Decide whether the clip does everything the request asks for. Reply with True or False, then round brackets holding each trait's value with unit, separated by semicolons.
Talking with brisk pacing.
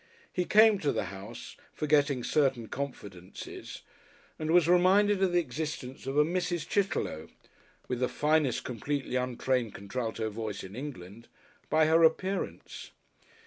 False (135 wpm)